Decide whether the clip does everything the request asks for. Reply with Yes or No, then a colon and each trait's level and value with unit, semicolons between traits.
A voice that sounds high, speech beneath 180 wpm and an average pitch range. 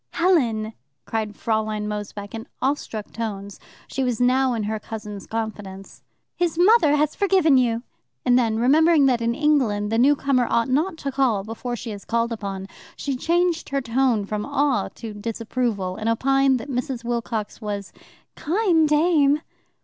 Yes: high, 240 Hz; average, 160 wpm; average, 4.6 semitones